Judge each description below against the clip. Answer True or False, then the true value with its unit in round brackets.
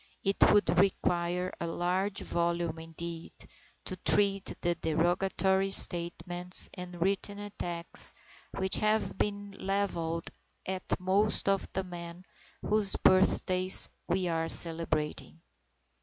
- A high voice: False (180 Hz)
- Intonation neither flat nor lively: False (2.3 semitones)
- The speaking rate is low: True (110 wpm)